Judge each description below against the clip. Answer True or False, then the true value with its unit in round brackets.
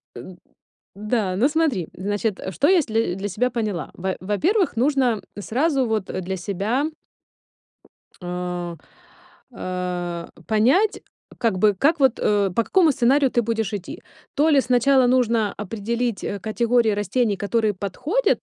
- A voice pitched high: True (220 Hz)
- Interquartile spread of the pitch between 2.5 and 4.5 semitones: False (5.0 semitones)